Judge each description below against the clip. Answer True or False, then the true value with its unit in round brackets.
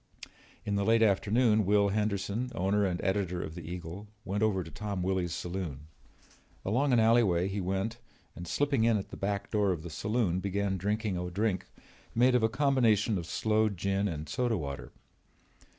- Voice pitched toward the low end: True (100 Hz)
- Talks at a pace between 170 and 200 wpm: True (180 wpm)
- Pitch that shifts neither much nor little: True (3.3 semitones)